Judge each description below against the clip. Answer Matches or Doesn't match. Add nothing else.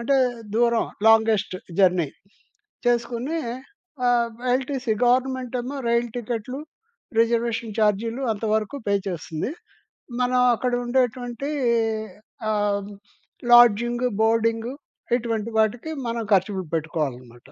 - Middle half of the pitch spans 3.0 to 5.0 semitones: Doesn't match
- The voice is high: Matches